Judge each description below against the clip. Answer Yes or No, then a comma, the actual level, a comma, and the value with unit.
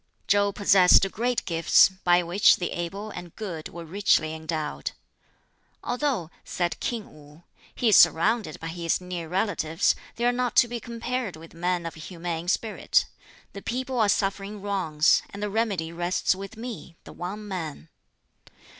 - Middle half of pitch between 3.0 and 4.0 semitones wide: No, average, 4.4 semitones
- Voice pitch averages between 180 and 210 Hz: Yes, medium, 185 Hz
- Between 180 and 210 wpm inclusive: No, average, 155 wpm